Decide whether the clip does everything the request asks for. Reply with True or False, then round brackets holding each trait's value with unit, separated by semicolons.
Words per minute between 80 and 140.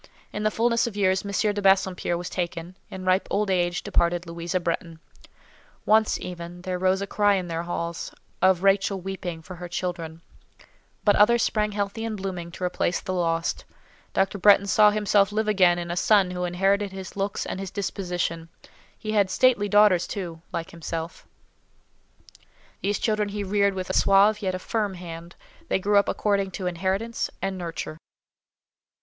False (175 wpm)